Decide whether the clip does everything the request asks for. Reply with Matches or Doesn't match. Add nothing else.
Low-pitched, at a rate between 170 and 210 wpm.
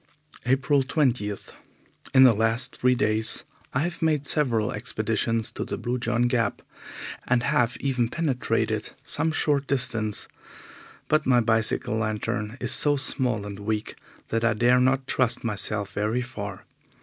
Doesn't match